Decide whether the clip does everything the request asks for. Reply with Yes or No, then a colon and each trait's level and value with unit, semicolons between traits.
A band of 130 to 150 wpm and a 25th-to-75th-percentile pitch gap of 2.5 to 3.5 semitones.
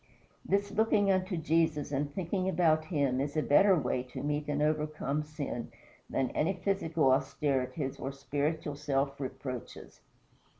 Yes: average, 140 wpm; average, 3.2 semitones